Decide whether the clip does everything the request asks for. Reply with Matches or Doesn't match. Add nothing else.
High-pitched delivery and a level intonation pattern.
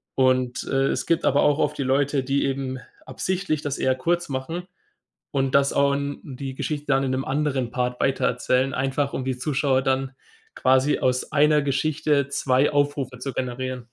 Doesn't match